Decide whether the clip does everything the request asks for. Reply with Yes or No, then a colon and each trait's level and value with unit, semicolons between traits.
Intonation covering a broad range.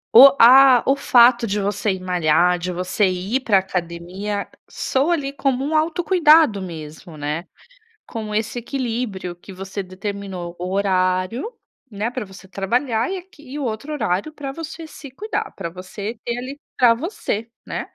Yes: wide, 6.6 semitones